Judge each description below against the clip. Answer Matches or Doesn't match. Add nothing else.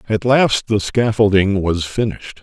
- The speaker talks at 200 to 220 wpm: Doesn't match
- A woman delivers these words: Doesn't match